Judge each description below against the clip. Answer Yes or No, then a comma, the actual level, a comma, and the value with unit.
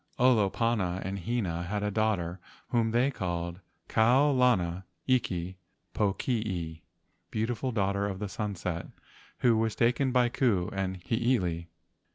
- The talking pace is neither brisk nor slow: No, slow, 120 wpm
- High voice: No, low, 105 Hz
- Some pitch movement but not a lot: Yes, average, 4.7 semitones